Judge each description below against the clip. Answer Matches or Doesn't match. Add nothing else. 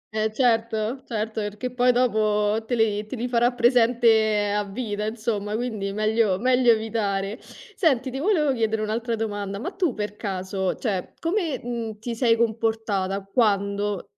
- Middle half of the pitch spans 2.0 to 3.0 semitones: Matches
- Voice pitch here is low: Doesn't match